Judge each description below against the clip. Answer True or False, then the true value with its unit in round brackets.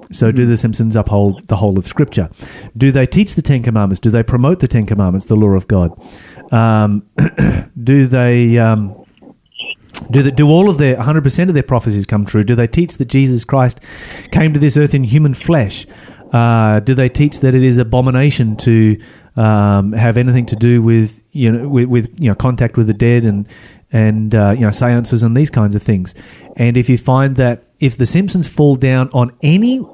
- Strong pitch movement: False (4.0 semitones)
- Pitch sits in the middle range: False (120 Hz)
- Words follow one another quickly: True (210 wpm)